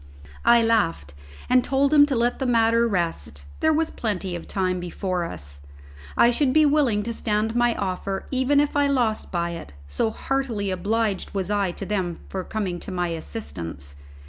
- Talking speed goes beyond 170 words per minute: Yes, average, 185 wpm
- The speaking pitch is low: No, high, 210 Hz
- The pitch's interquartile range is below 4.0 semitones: No, wide, 5.4 semitones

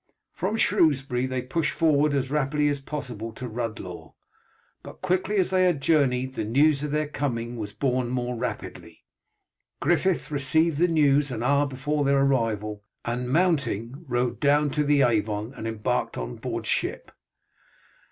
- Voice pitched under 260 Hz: Yes, low, 135 Hz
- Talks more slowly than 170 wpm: Yes, average, 155 wpm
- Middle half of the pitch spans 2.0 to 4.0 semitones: Yes, average, 3.6 semitones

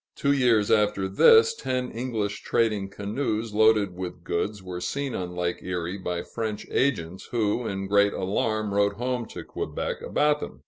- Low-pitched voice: Yes, low, 105 Hz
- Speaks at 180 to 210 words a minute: No, average, 165 wpm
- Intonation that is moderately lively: Yes, average, 3.8 semitones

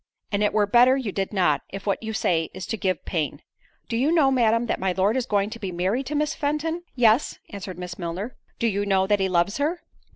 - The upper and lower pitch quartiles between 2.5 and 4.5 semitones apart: No, average, 4.9 semitones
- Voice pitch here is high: Yes, high, 210 Hz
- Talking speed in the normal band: No, fast, 240 wpm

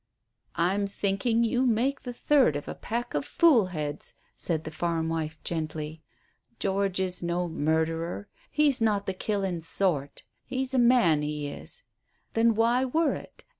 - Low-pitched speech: No, high, 190 Hz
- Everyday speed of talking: Yes, average, 150 wpm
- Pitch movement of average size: No, wide, 6.7 semitones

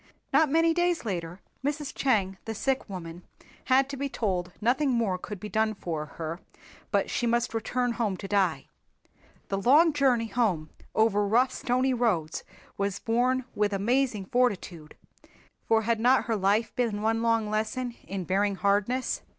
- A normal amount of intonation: Yes, average, 4.3 semitones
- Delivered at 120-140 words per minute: No, average, 160 wpm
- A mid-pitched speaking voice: No, high, 225 Hz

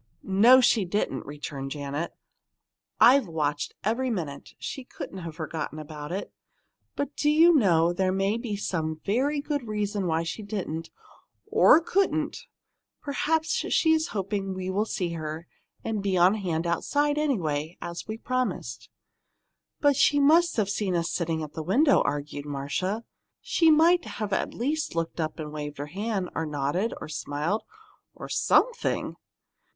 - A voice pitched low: No, high, 195 Hz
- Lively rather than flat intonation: Yes, wide, 8.1 semitones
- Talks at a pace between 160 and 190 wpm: No, average, 150 wpm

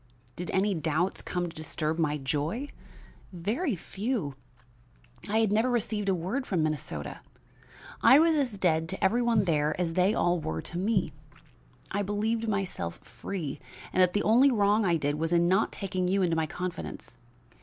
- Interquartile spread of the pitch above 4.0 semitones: Yes, average, 4.6 semitones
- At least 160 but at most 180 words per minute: Yes, average, 175 wpm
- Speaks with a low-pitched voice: No, medium, 185 Hz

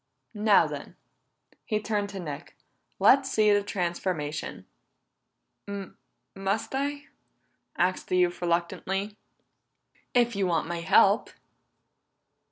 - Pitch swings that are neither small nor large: Yes, average, 3.4 semitones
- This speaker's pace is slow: Yes, slow, 100 wpm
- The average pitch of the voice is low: No, high, 195 Hz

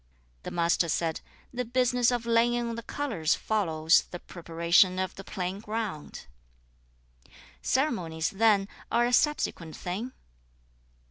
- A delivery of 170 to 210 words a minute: No, average, 140 wpm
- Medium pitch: No, high, 195 Hz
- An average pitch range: No, wide, 5.9 semitones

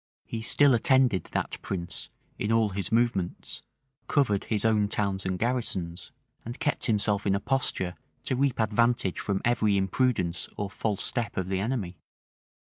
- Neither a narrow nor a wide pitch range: Yes, average, 3.9 semitones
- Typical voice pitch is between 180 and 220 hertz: No, low, 105 Hz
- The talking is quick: No, average, 155 wpm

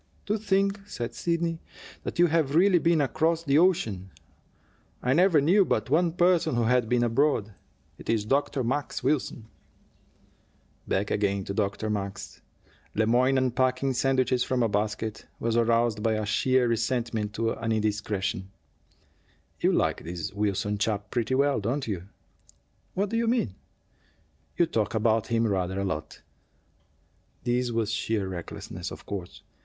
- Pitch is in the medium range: No, low, 120 Hz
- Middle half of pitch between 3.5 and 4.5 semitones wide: No, wide, 5.4 semitones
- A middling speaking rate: Yes, average, 150 wpm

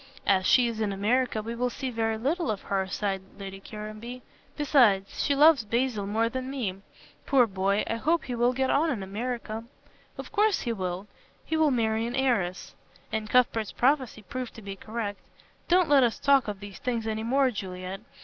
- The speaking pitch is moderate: No, high, 230 Hz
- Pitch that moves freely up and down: No, average, 4.2 semitones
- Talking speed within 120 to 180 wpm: No, average, 195 wpm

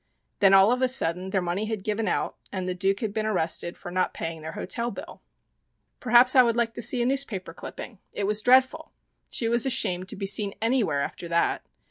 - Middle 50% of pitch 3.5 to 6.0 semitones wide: Yes, average, 4.6 semitones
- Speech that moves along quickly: Yes, fast, 215 wpm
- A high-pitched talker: Yes, high, 210 Hz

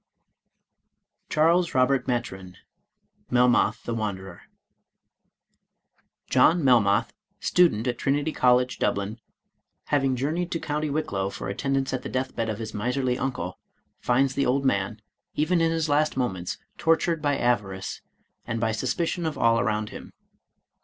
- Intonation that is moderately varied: Yes, average, 4.9 semitones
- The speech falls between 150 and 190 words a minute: No, average, 140 wpm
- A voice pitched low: Yes, low, 125 Hz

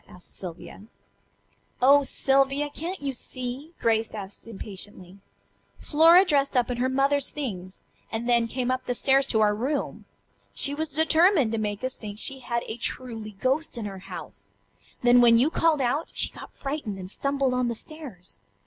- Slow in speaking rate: No, average, 175 wpm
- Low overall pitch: No, very high, 250 Hz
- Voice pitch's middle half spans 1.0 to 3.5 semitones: No, average, 4.4 semitones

